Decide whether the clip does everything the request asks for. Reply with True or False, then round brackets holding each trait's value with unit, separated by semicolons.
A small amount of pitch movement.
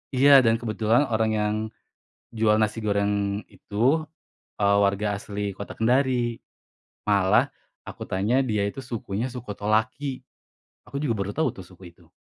False (3.4 semitones)